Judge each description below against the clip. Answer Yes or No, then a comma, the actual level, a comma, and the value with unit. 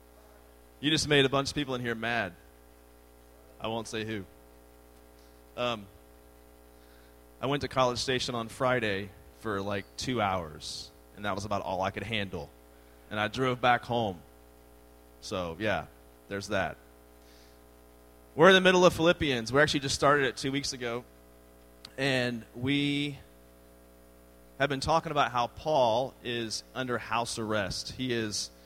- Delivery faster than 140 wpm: Yes, average, 150 wpm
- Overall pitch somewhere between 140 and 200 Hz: No, low, 100 Hz